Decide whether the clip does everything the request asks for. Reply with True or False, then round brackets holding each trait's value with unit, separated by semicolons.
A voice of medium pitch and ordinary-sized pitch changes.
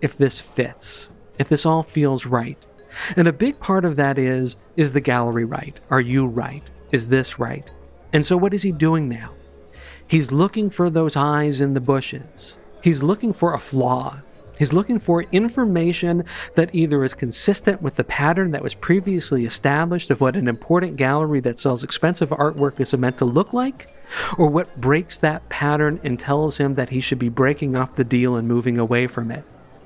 True (145 Hz; 4.6 semitones)